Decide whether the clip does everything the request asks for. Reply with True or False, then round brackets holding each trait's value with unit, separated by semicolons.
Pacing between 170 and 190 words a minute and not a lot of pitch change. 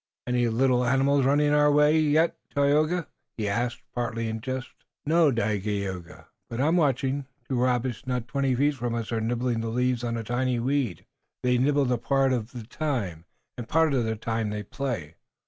False (185 wpm; 3.6 semitones)